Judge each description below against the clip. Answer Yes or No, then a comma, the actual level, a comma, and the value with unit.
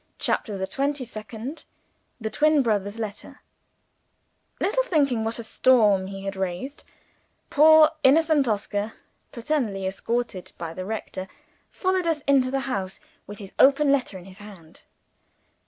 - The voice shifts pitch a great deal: Yes, wide, 6.2 semitones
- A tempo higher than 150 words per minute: No, average, 140 wpm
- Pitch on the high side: Yes, high, 225 Hz